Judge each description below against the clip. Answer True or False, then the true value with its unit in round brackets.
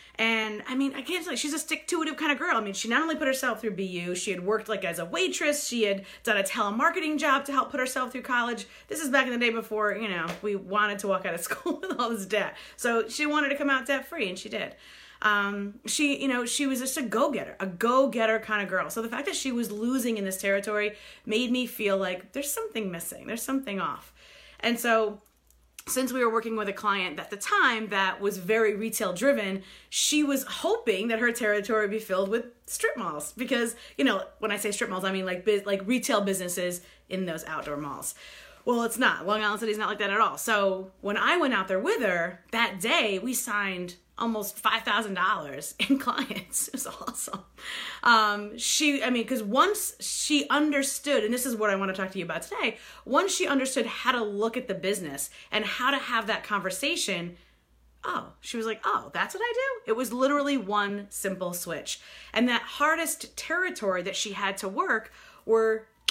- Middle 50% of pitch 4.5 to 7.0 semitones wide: True (4.8 semitones)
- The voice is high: True (225 Hz)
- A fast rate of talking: True (220 wpm)